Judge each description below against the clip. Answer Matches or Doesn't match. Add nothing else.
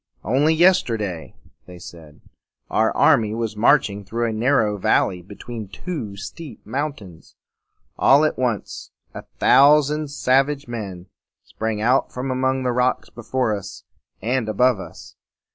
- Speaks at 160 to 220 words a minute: Doesn't match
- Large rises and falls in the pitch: Doesn't match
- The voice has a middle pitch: Doesn't match